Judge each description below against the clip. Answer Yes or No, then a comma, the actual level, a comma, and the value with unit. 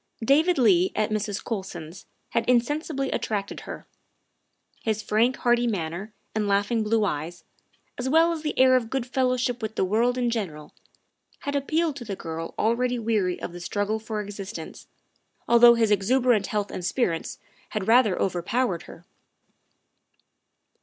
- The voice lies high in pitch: Yes, high, 220 Hz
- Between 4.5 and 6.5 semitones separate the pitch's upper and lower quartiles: No, average, 4.1 semitones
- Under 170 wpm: Yes, average, 155 wpm